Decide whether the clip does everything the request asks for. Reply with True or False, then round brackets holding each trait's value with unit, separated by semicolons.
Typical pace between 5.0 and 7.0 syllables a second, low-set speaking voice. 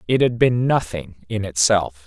False (4.3 syllables/s; 105 Hz)